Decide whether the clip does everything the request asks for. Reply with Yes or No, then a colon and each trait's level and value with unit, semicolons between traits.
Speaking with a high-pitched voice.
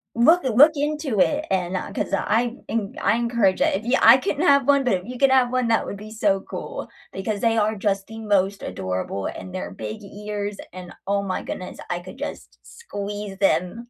Yes: high, 210 Hz